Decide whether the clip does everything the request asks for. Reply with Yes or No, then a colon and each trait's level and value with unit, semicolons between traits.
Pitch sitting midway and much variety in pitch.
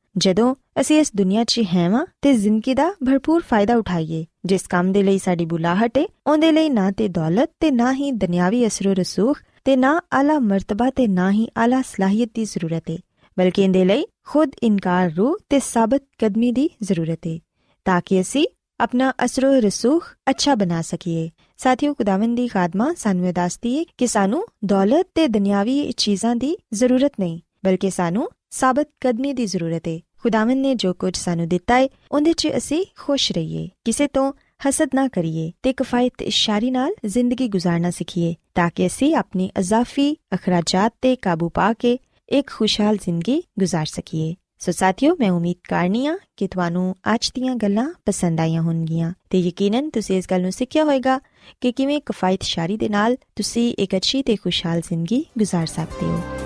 No: high, 215 Hz; wide, 6.3 semitones